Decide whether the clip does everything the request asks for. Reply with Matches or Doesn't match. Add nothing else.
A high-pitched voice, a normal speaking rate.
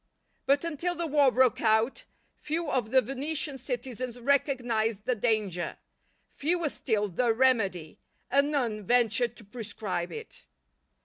Doesn't match